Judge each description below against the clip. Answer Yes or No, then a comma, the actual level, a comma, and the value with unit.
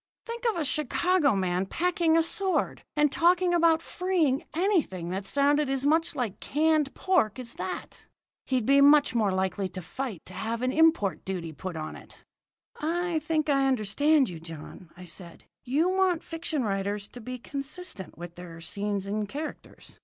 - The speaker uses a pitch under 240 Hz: No, very high, 270 Hz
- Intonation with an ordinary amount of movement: No, wide, 8.7 semitones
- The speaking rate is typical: Yes, average, 170 wpm